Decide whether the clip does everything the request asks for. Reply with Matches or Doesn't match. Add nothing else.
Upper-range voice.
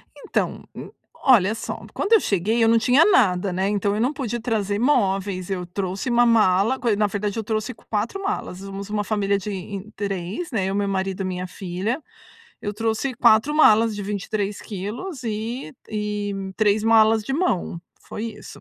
Matches